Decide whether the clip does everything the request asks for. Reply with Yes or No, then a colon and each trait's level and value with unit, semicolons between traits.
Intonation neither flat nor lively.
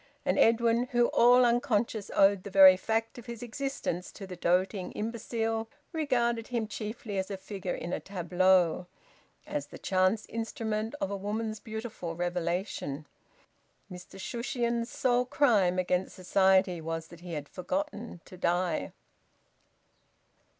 Yes: average, 4.3 semitones